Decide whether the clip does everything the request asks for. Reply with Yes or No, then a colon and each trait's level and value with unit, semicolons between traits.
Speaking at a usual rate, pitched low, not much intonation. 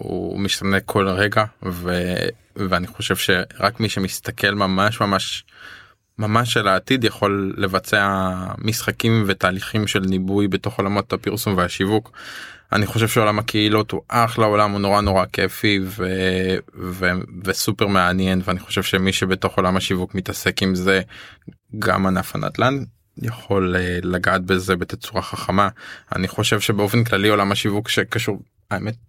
Yes: average, 135 wpm; low, 100 Hz; narrow, 2.1 semitones